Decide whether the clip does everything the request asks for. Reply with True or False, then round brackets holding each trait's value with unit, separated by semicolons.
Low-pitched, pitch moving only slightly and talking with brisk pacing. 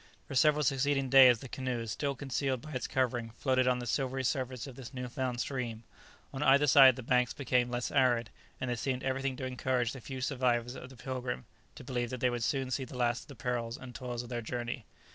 True (130 Hz; 1.5 semitones; 230 wpm)